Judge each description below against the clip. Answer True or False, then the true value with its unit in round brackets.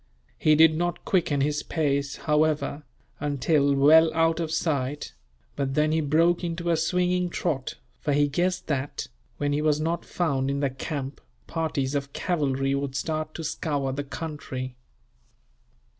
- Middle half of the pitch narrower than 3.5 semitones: True (2.7 semitones)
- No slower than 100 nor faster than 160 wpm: True (155 wpm)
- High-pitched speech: False (150 Hz)